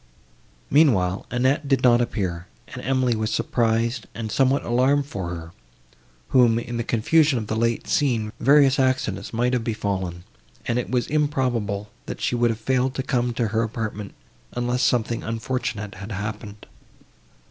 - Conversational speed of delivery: Yes, average, 160 wpm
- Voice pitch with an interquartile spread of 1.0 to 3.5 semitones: Yes, average, 3.2 semitones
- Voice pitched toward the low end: Yes, low, 115 Hz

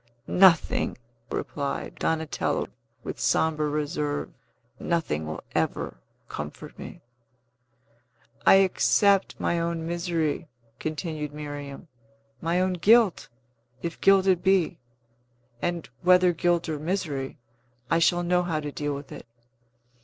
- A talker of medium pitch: Yes, medium, 165 Hz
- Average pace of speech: No, slow, 115 wpm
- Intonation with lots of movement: No, average, 3.1 semitones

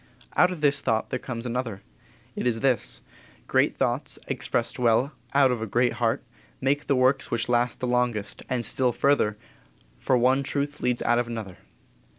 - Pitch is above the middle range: No, low, 125 Hz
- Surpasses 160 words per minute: Yes, average, 175 wpm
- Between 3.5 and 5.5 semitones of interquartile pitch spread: No, narrow, 2.4 semitones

